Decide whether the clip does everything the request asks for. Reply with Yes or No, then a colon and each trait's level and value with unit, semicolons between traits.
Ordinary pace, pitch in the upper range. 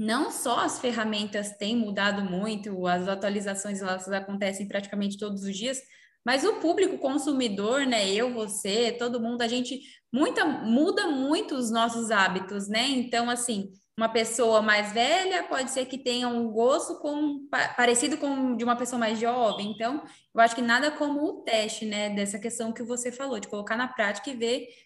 Yes: average, 175 wpm; high, 235 Hz